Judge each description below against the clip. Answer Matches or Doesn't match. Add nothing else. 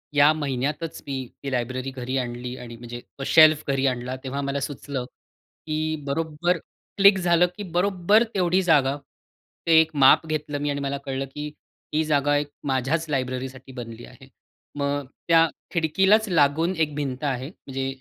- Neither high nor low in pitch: Matches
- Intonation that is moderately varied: Matches